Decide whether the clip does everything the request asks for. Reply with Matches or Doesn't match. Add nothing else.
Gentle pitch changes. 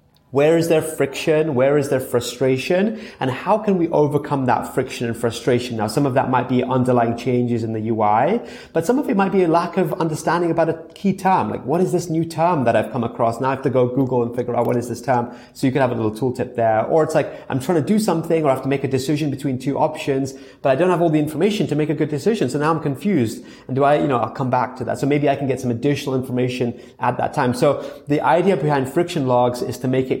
Doesn't match